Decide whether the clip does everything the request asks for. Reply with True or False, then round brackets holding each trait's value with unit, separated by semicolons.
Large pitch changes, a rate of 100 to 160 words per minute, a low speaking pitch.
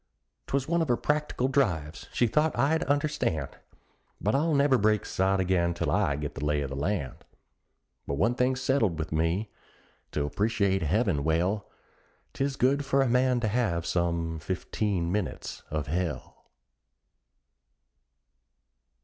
True (7.8 semitones; 145 wpm; 100 Hz)